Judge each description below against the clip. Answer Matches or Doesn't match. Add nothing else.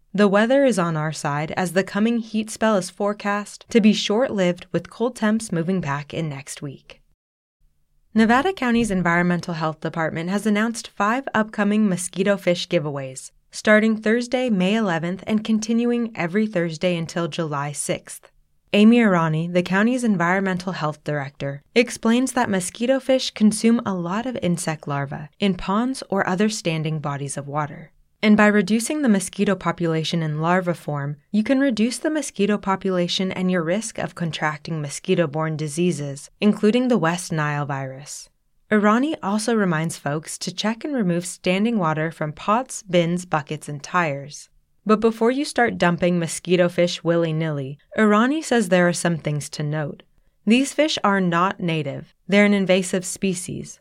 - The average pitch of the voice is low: Doesn't match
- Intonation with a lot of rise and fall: Doesn't match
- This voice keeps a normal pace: Matches